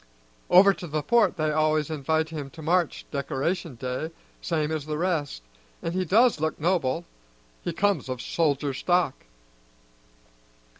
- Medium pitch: Yes, medium, 155 Hz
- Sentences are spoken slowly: No, average, 145 wpm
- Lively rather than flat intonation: No, average, 3.3 semitones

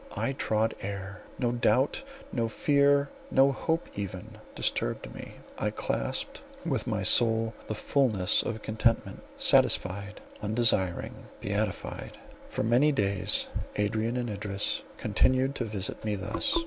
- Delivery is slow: Yes, slow, 125 wpm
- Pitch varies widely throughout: No, average, 3.7 semitones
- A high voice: No, low, 110 Hz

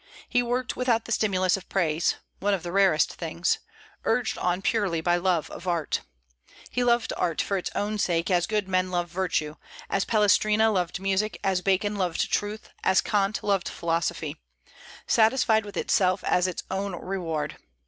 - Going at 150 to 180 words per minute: Yes, average, 170 wpm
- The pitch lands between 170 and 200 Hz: Yes, high, 190 Hz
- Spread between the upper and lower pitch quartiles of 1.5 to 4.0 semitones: Yes, average, 3.3 semitones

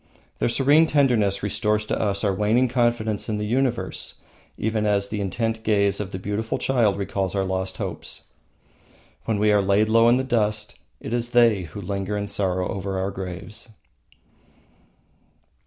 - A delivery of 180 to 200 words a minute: No, average, 165 wpm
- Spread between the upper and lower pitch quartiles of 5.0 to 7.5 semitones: No, narrow, 2.6 semitones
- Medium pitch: No, low, 105 Hz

